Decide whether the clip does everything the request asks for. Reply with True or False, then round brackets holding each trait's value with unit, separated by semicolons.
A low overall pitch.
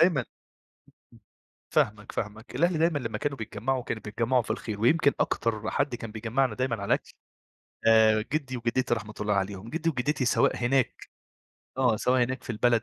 True (120 Hz)